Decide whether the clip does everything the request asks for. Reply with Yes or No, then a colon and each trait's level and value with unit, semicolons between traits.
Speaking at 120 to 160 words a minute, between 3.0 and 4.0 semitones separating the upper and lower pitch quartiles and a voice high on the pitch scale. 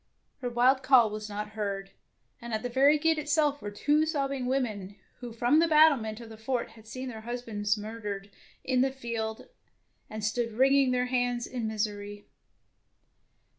No: average, 170 wpm; average, 3.6 semitones; high, 240 Hz